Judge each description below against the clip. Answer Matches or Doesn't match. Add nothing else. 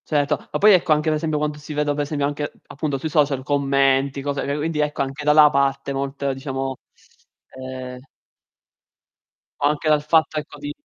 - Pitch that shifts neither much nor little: Doesn't match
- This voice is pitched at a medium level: Matches